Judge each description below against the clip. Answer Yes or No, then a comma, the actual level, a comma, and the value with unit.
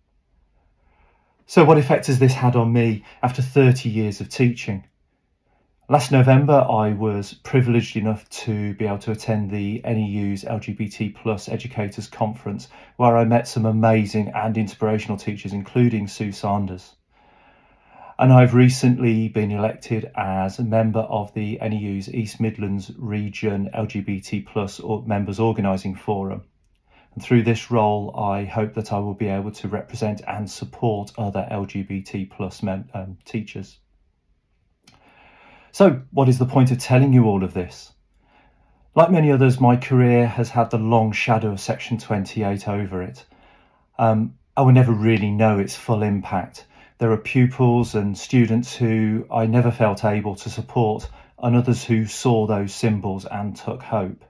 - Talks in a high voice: No, low, 110 Hz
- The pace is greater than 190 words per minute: No, average, 150 wpm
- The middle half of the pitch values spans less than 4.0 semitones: Yes, average, 2.8 semitones